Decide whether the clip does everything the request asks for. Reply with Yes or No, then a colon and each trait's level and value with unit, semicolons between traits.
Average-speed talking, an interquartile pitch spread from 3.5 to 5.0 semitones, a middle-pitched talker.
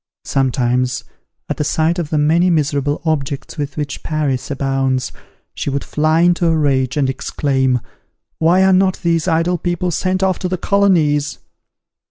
Yes: average, 160 wpm; average, 4.0 semitones; medium, 155 Hz